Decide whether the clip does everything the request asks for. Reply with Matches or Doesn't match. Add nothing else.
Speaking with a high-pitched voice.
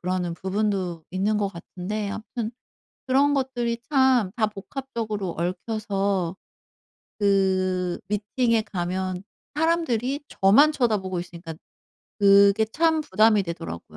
Matches